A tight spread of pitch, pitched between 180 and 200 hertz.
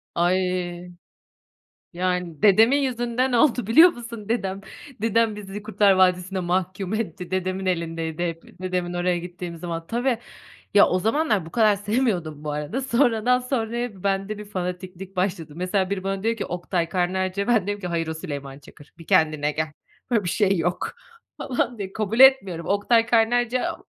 No: average, 4.2 semitones; high, 190 Hz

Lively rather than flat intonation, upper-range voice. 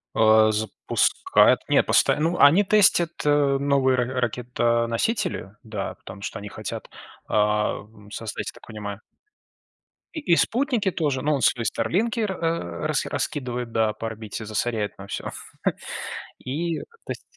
No: wide, 6.8 semitones; low, 120 Hz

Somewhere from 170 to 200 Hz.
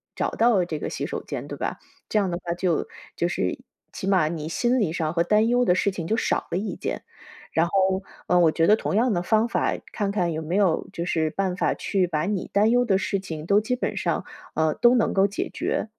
Yes: high, 190 Hz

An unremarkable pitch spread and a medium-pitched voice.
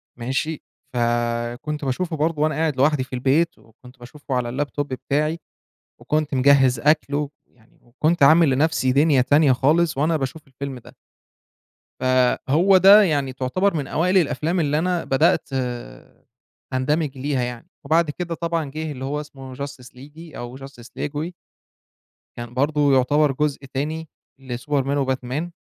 Yes: average, 3.3 semitones; medium, 145 Hz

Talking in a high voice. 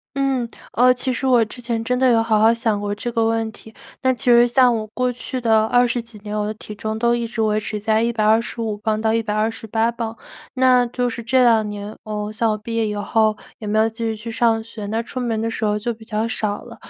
Yes: high, 225 Hz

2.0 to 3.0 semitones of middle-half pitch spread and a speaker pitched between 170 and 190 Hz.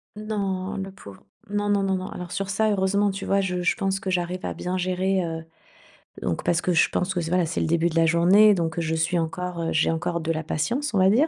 Yes: narrow, 2.6 semitones; medium, 185 Hz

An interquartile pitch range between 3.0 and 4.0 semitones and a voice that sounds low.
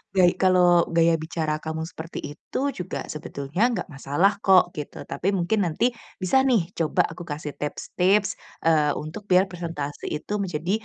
No: average, 3.3 semitones; medium, 170 Hz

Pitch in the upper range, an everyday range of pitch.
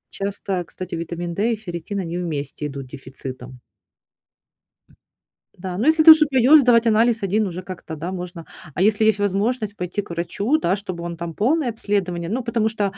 Yes: high, 195 Hz; average, 4.5 semitones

